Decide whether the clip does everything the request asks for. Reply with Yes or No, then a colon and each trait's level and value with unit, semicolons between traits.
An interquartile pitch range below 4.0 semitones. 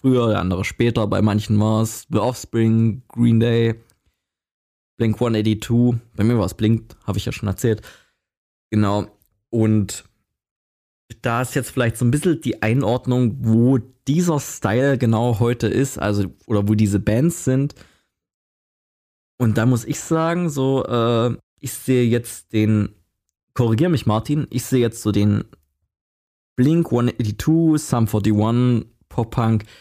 Yes: average, 2.9 semitones